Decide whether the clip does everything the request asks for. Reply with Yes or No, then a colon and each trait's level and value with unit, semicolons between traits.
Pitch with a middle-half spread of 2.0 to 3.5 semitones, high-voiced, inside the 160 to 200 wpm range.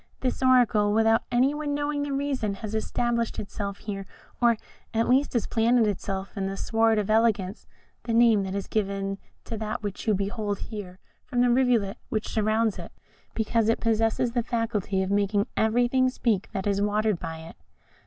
Yes: average, 3.0 semitones; high, 220 Hz; average, 180 wpm